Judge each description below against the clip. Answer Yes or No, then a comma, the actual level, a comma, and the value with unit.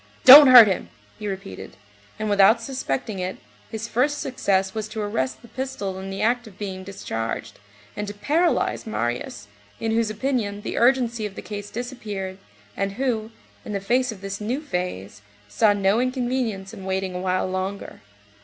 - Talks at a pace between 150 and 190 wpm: Yes, average, 170 wpm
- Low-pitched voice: No, high, 210 Hz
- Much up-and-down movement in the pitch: No, average, 3.9 semitones